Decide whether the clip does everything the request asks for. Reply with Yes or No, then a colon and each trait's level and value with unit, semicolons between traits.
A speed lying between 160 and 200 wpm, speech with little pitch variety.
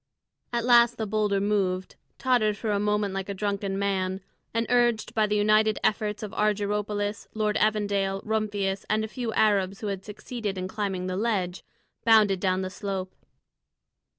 Yes: average, 165 wpm; narrow, 1.8 semitones